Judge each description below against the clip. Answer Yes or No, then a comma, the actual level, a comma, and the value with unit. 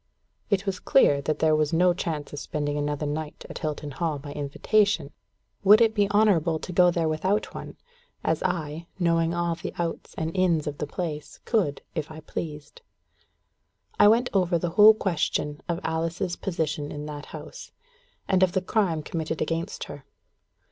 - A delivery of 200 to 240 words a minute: No, average, 175 wpm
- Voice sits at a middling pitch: Yes, medium, 165 Hz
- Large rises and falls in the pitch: No, average, 3.6 semitones